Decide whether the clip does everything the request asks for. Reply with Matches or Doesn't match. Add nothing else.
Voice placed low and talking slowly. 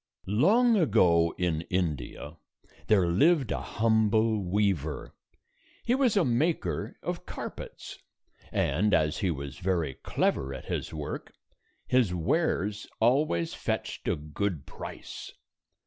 Matches